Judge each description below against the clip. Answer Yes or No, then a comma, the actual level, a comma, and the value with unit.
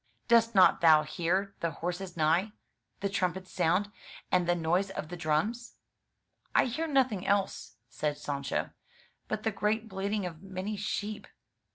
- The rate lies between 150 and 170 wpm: Yes, average, 155 wpm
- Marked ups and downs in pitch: No, average, 3.8 semitones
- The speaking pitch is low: No, high, 190 Hz